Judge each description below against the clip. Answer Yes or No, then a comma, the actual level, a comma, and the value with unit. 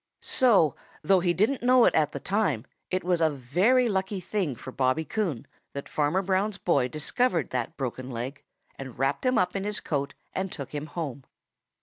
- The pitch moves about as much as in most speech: No, wide, 6.2 semitones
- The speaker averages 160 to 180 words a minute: No, average, 190 wpm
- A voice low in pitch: No, medium, 170 Hz